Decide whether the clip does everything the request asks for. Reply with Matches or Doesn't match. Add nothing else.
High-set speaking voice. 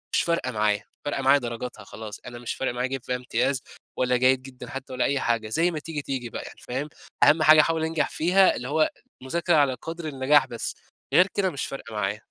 Doesn't match